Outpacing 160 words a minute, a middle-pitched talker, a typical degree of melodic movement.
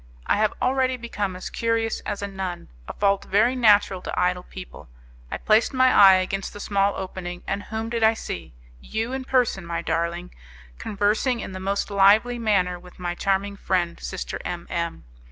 No: average, 185 wpm; high, 200 Hz; average, 3.5 semitones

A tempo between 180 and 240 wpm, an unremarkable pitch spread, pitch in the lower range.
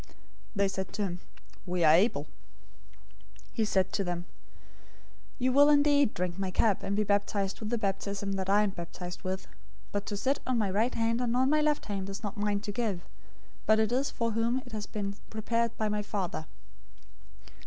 No: average, 195 wpm; average, 3.1 semitones; high, 205 Hz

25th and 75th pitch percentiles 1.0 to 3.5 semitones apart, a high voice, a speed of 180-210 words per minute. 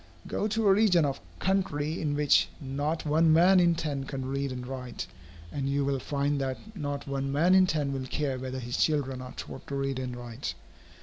No: average, 3.1 semitones; medium, 140 Hz; fast, 205 wpm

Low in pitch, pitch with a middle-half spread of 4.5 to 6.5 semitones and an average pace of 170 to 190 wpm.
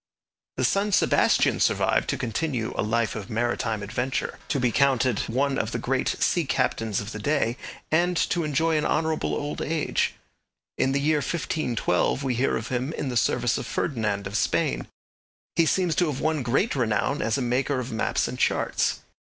Yes: low, 130 Hz; average, 4.9 semitones; average, 185 wpm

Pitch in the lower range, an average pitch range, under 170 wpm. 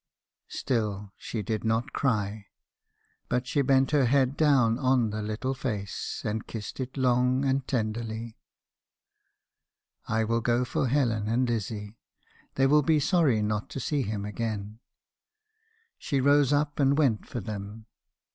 Yes: low, 120 Hz; average, 3.8 semitones; average, 150 wpm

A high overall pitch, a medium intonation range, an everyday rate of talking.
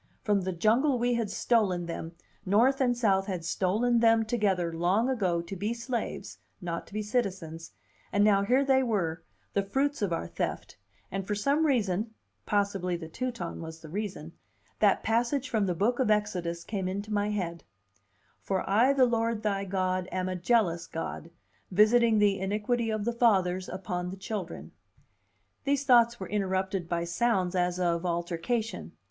Yes: high, 200 Hz; average, 4.4 semitones; average, 170 wpm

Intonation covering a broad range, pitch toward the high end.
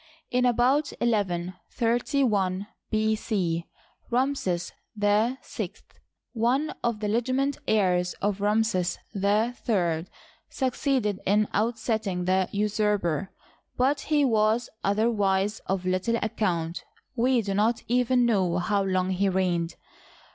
No: average, 4.1 semitones; high, 210 Hz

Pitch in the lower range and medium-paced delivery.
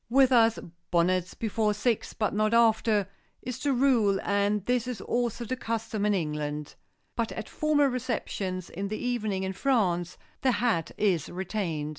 No: high, 215 Hz; average, 160 wpm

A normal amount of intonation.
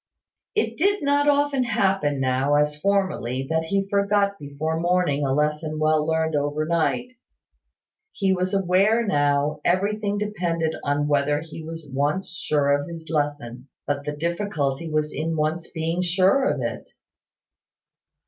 Yes: average, 4.8 semitones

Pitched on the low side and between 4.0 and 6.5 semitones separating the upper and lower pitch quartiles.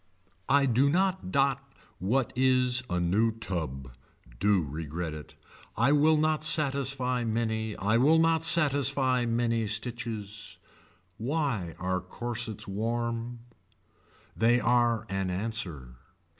Yes: low, 115 Hz; average, 5.2 semitones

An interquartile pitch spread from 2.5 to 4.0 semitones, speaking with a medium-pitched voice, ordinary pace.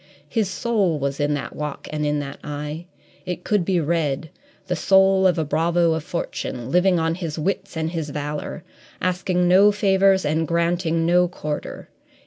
Yes: average, 3.6 semitones; medium, 170 Hz; average, 170 wpm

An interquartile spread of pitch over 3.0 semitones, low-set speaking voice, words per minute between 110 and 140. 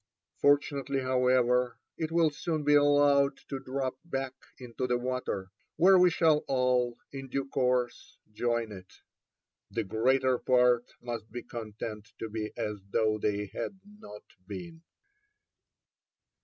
Yes: average, 3.4 semitones; low, 125 Hz; slow, 135 wpm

